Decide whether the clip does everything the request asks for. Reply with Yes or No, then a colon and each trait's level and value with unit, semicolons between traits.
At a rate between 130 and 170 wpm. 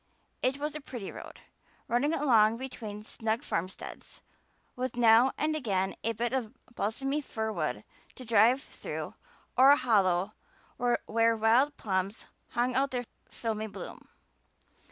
Yes: slow, 135 wpm